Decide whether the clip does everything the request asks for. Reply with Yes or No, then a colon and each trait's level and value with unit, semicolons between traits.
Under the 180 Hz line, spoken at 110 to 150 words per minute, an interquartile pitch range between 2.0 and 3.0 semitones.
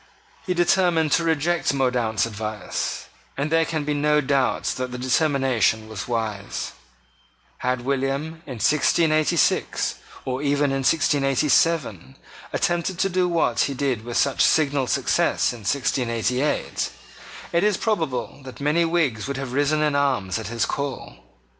No: medium, 140 Hz; average, 140 wpm; average, 4.1 semitones